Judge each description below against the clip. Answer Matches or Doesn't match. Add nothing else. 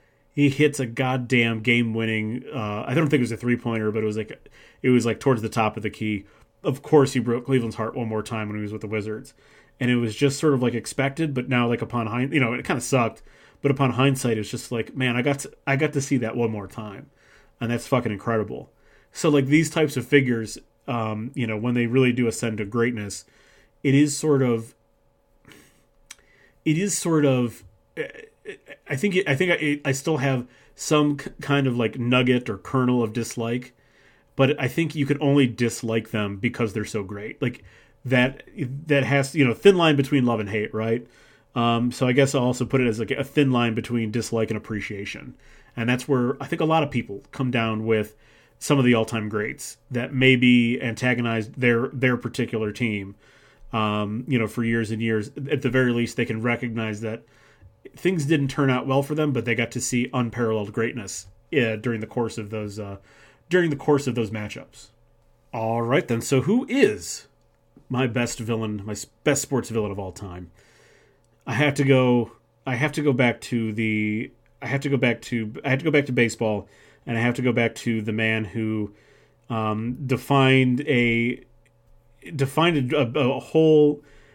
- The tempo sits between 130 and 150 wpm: Doesn't match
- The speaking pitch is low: Matches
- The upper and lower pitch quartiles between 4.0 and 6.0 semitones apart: Doesn't match